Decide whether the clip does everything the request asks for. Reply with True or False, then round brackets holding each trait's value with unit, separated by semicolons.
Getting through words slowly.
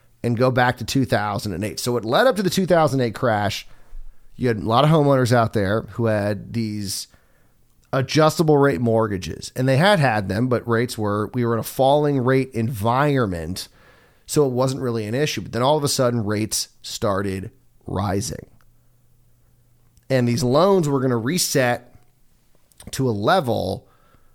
False (165 wpm)